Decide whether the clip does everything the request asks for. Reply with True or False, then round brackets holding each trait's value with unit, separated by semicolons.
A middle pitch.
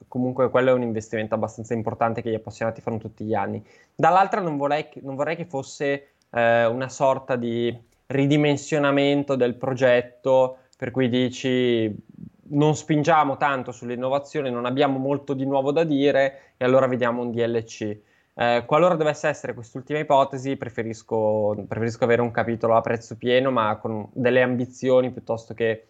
False (125 Hz)